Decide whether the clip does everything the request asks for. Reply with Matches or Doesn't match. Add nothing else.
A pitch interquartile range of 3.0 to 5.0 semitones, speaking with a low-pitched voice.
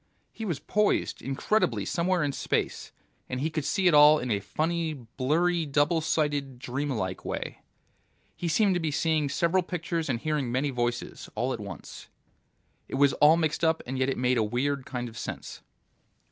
Doesn't match